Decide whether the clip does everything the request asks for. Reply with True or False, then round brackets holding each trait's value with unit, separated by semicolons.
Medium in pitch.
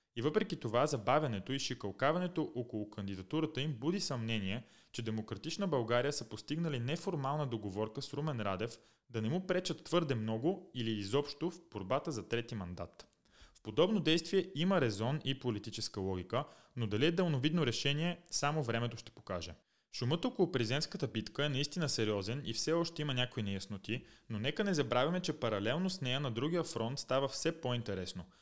False (130 Hz)